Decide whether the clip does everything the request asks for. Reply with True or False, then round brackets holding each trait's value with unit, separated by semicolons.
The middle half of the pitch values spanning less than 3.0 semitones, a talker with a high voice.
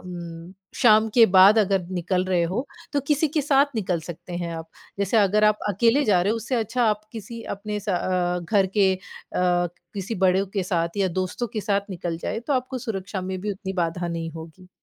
False (3.7 semitones; 195 Hz)